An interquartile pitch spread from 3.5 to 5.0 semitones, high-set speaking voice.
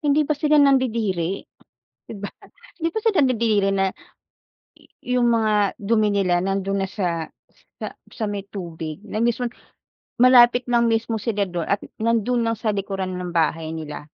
Yes: average, 3.9 semitones; high, 210 Hz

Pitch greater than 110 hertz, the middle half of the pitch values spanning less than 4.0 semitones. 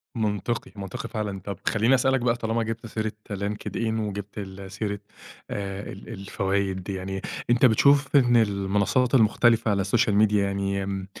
No: low, 105 Hz; average, 2.8 semitones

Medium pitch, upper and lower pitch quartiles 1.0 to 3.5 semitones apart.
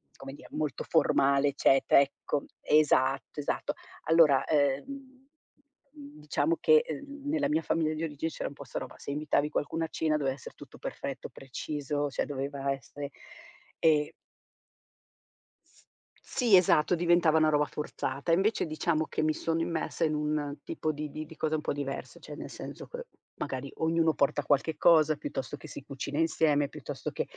Yes: medium, 150 Hz; narrow, 2.4 semitones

